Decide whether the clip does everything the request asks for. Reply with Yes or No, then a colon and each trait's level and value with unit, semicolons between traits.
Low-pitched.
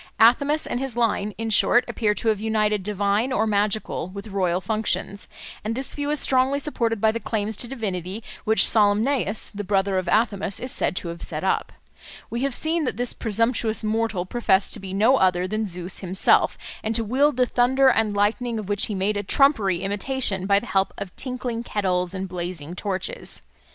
No: high, 215 Hz